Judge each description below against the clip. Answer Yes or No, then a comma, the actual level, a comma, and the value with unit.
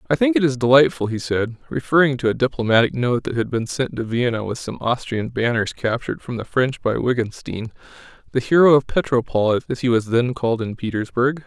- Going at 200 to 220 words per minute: Yes, fast, 205 wpm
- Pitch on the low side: Yes, low, 120 Hz